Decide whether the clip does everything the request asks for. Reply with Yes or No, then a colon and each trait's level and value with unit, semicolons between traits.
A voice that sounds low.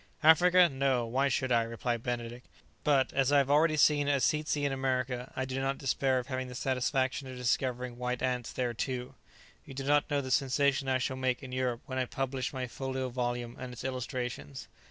Yes: low, 130 Hz